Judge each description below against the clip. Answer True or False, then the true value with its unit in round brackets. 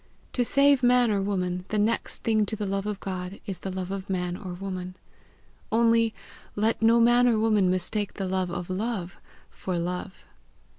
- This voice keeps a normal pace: True (185 wpm)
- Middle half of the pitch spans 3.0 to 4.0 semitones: True (3.5 semitones)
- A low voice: False (195 Hz)